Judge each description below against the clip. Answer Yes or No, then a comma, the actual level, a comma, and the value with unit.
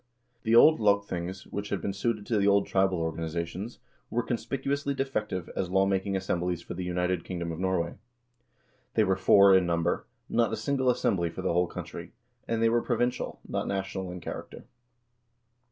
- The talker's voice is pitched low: Yes, very low, 95 Hz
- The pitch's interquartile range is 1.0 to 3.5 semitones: No, average, 3.9 semitones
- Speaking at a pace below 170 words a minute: No, average, 175 wpm